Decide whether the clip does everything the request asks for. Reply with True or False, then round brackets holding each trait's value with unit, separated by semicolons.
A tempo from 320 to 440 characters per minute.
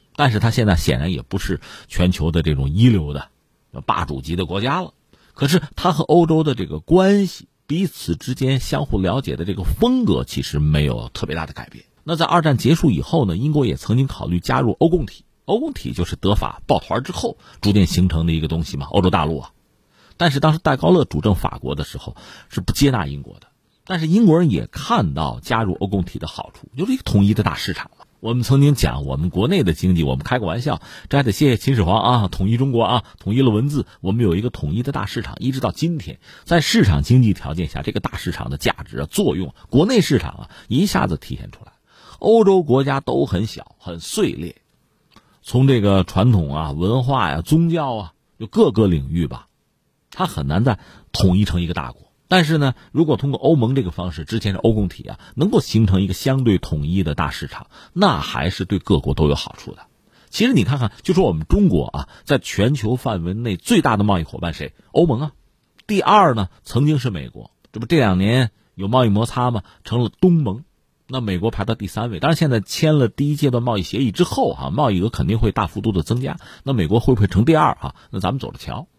True (325 characters per minute)